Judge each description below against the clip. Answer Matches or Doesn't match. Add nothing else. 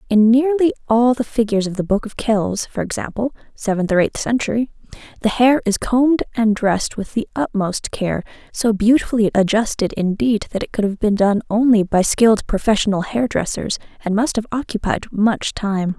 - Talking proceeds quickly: Doesn't match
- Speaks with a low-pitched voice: Doesn't match